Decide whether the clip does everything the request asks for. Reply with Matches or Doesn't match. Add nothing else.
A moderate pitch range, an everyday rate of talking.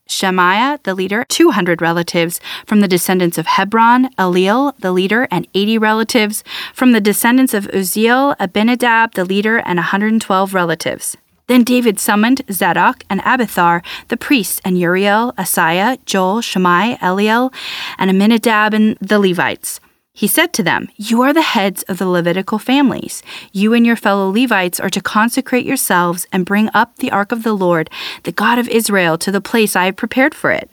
Matches